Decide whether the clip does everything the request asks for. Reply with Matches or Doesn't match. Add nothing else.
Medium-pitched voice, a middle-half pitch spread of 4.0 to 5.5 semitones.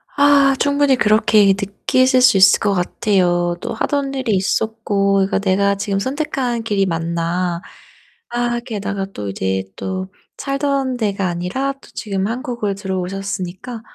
Doesn't match